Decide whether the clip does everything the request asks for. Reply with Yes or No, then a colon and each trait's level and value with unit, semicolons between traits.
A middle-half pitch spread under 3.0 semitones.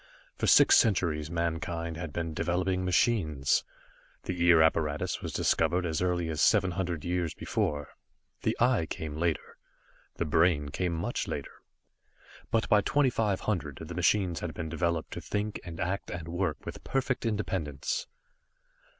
Yes: narrow, 2.6 semitones